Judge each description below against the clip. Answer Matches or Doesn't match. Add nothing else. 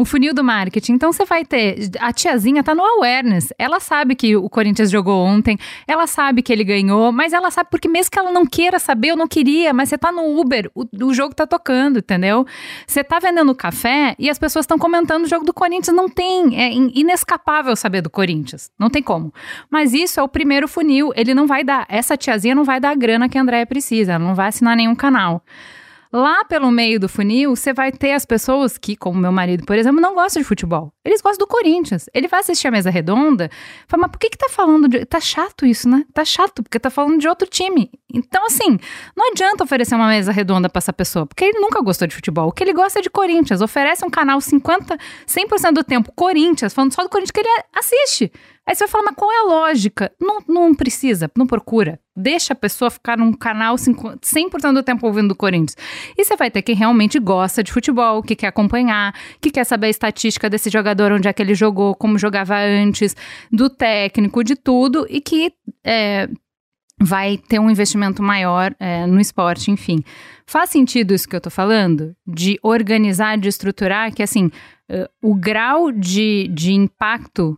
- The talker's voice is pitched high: Matches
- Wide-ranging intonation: Matches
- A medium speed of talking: Doesn't match